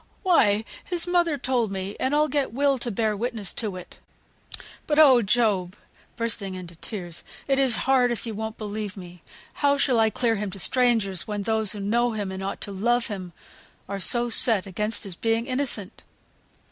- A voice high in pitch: Yes, high, 220 Hz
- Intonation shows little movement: No, average, 3.9 semitones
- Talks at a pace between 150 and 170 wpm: No, average, 185 wpm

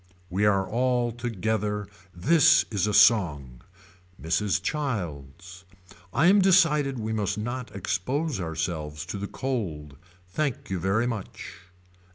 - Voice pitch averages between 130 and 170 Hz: No, low, 105 Hz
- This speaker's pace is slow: Yes, slow, 125 wpm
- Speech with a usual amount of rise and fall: No, wide, 5.7 semitones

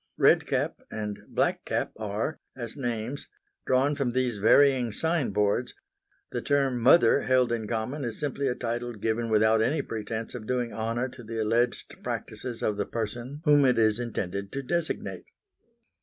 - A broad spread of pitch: No, average, 3.0 semitones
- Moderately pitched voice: No, low, 120 Hz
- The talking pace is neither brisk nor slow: Yes, average, 165 wpm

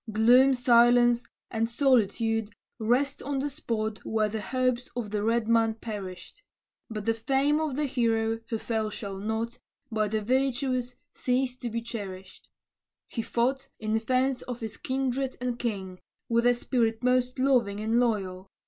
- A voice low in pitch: No, high, 235 Hz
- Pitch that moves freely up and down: No, narrow, 2.6 semitones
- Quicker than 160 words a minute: No, average, 155 wpm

